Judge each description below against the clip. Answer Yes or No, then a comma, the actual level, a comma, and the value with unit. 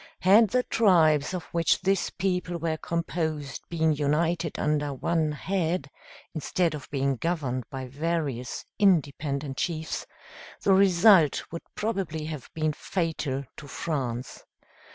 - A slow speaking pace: Yes, slow, 125 wpm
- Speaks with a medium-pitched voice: Yes, medium, 160 Hz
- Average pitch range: Yes, average, 3.5 semitones